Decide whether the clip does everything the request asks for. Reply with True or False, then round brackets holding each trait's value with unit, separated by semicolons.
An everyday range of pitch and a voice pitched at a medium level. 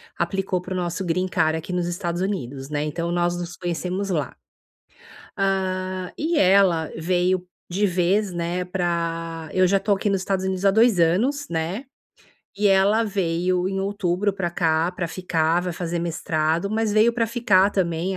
False (2.3 semitones; 180 Hz)